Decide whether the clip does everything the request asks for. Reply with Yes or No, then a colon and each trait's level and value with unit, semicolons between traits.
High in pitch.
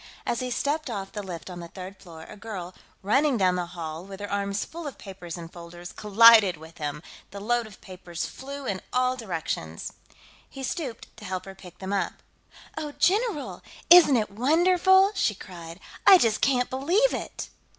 Yes: high, 205 Hz